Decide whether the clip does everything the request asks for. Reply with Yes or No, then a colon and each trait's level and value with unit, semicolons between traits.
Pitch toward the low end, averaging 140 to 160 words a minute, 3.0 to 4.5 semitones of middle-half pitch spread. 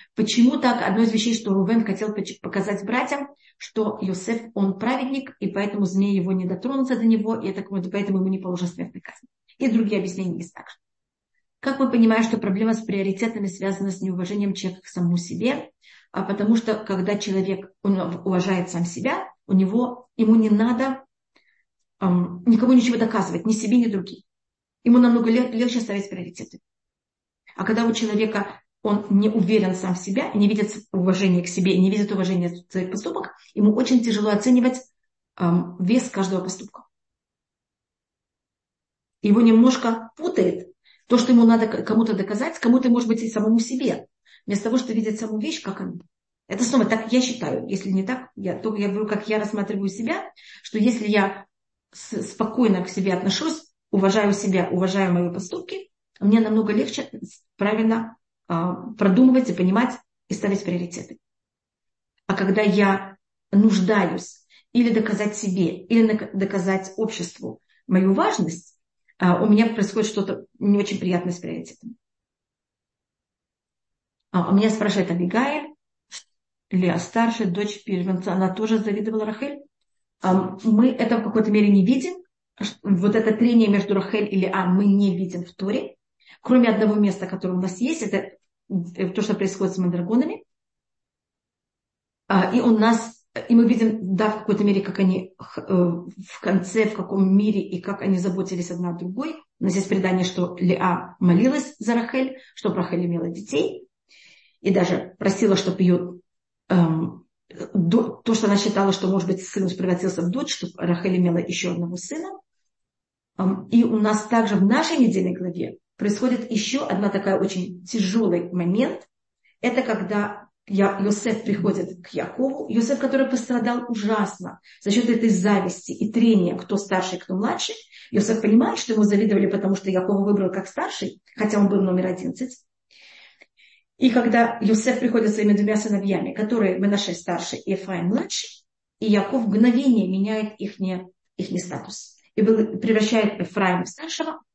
No: high, 205 Hz; average, 150 wpm; average, 3.3 semitones